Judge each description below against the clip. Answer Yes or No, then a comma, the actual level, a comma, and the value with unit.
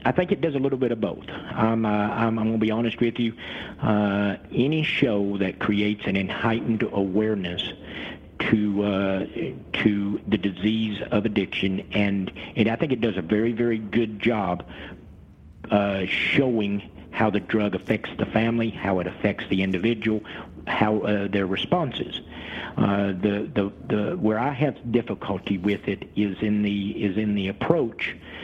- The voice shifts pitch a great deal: No, narrow, 2.4 semitones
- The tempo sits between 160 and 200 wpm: Yes, average, 165 wpm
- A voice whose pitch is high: No, low, 105 Hz